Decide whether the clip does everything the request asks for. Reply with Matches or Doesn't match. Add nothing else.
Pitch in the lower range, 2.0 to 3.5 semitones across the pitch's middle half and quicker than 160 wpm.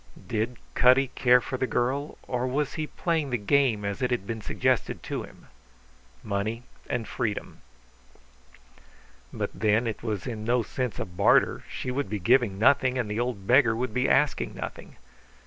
Matches